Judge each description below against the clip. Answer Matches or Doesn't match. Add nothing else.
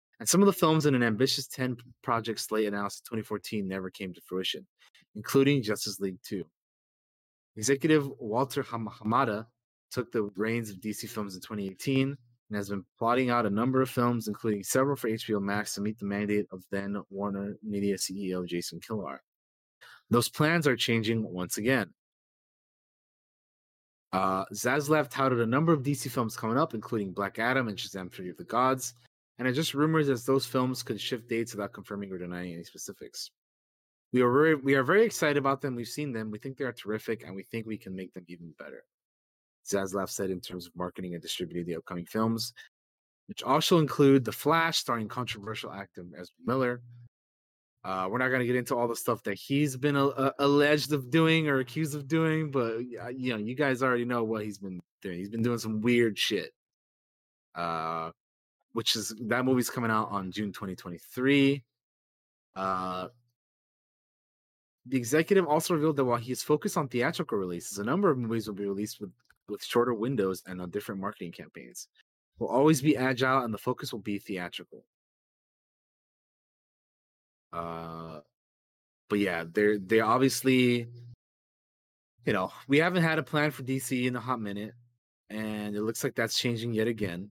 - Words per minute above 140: Matches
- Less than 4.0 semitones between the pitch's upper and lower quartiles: Doesn't match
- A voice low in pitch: Matches